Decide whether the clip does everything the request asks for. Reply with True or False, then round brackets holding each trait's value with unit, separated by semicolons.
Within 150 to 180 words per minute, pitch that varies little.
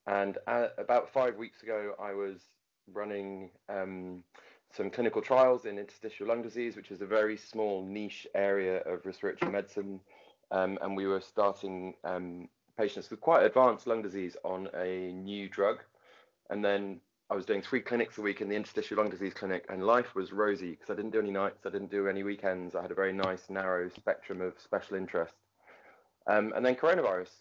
False (190 wpm; 2.0 semitones)